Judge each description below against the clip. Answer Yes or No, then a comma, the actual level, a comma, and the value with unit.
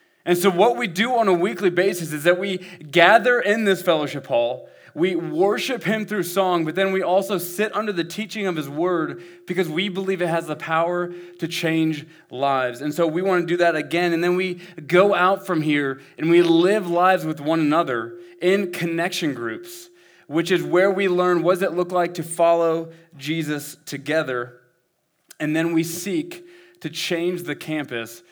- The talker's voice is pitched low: No, medium, 175 Hz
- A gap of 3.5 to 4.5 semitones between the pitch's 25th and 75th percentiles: No, average, 2.8 semitones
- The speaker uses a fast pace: No, average, 190 wpm